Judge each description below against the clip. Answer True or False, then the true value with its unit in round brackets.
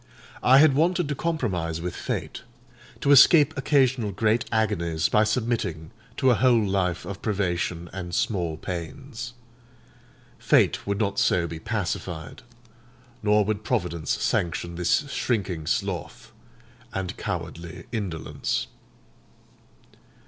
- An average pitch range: False (5.8 semitones)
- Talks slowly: True (115 wpm)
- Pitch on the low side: True (100 Hz)